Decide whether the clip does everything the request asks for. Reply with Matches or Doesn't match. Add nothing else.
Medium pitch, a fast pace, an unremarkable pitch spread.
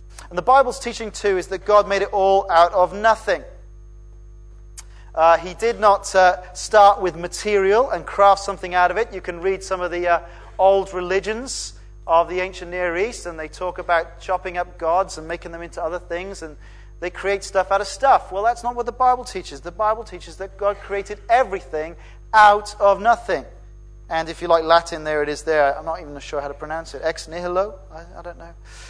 Matches